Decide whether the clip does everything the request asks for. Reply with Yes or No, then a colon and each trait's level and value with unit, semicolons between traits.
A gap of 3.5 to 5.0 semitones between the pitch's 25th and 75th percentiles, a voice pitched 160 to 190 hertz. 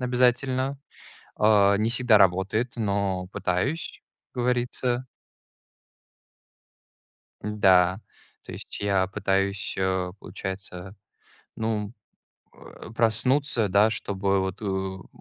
No: average, 4.1 semitones; low, 100 Hz